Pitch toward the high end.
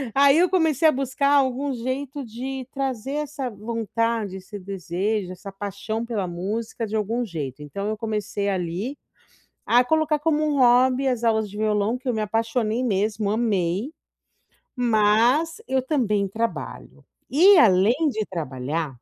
Yes: high, 225 Hz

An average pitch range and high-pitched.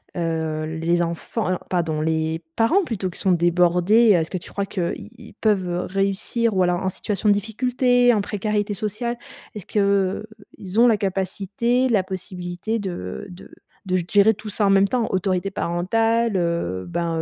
Yes: average, 3.7 semitones; high, 195 Hz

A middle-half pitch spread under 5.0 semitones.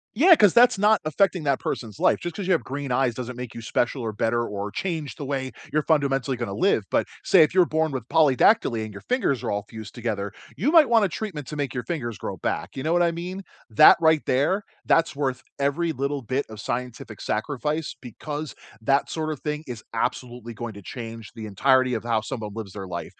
No: wide, 5.6 semitones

